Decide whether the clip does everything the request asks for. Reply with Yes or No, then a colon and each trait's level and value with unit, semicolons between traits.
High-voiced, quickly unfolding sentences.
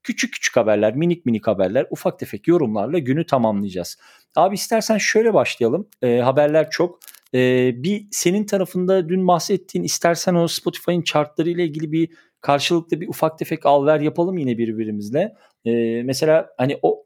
No: medium, 165 Hz; fast, 155 wpm